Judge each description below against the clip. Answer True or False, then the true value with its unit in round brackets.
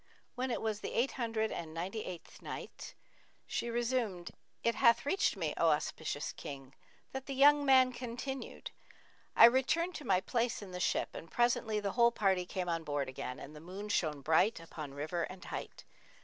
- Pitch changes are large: True (6.6 semitones)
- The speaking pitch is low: False (210 Hz)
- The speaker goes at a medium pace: True (185 wpm)